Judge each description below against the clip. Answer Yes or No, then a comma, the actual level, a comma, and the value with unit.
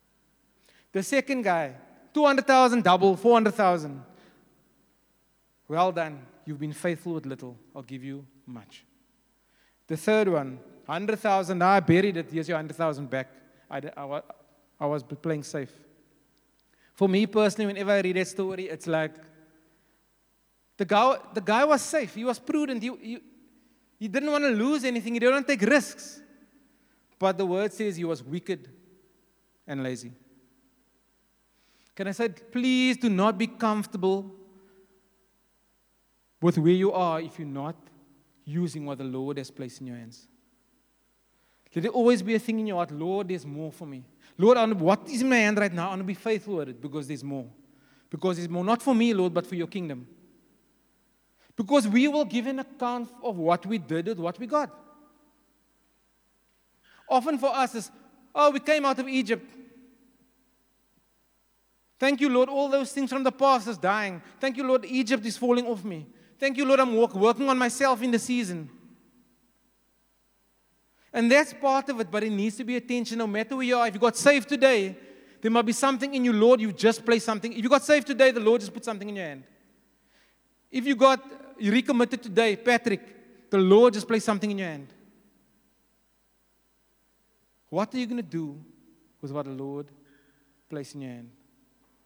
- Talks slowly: No, average, 175 wpm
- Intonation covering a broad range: Yes, wide, 7.7 semitones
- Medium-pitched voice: No, high, 210 Hz